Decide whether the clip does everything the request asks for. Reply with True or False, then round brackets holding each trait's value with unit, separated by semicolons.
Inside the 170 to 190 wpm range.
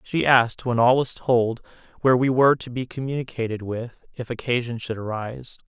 True (180 wpm)